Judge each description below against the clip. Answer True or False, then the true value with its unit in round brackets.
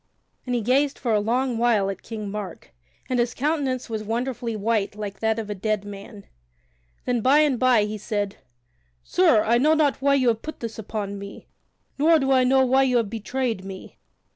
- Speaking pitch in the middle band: False (230 Hz)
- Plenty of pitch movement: False (3.7 semitones)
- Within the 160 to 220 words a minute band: True (200 wpm)